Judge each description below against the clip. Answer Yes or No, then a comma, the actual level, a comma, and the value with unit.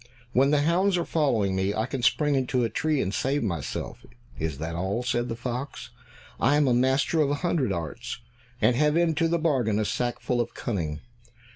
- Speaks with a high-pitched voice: No, low, 125 Hz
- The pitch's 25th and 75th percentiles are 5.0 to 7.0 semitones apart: Yes, wide, 5.5 semitones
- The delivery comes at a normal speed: Yes, average, 190 wpm